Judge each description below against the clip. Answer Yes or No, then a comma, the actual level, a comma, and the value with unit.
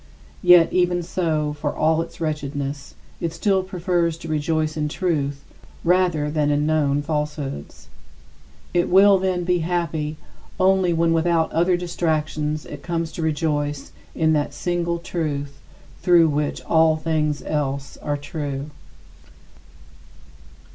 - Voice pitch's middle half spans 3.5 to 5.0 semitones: No, narrow, 2.6 semitones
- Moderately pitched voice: Yes, medium, 160 Hz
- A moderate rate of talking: No, slow, 125 wpm